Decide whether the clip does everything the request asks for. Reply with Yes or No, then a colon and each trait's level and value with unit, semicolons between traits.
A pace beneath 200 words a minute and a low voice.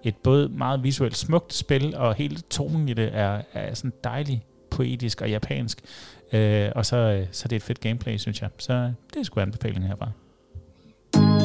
Yes: average, 185 wpm; low, 115 Hz